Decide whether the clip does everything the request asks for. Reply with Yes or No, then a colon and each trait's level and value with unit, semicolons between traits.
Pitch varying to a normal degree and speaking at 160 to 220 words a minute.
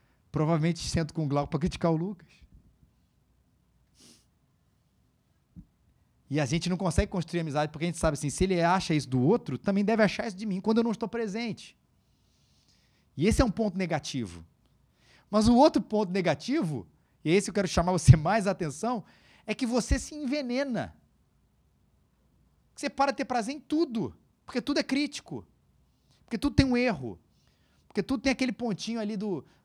No: wide, 6.4 semitones; average, 175 wpm